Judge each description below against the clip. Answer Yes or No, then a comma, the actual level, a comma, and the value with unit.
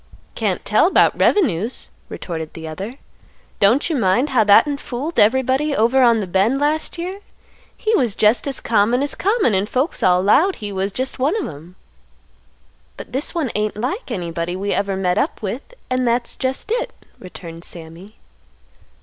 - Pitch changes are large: Yes, wide, 6.5 semitones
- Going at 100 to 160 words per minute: No, average, 175 wpm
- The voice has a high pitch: Yes, high, 230 Hz